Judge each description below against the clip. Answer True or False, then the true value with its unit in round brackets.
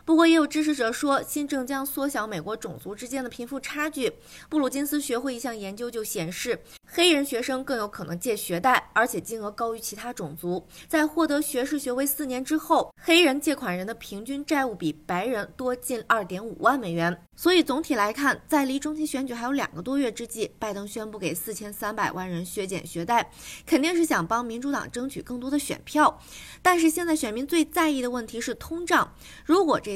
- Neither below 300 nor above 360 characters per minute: True (315 characters per minute)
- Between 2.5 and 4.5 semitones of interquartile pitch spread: False (5.4 semitones)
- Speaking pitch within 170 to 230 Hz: False (255 Hz)